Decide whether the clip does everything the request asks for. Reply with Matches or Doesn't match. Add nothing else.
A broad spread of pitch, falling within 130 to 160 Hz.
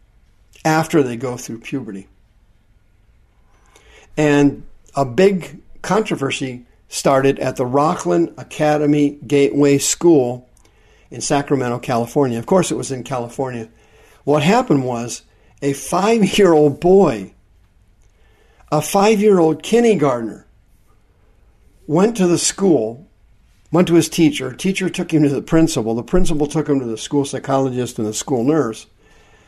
Matches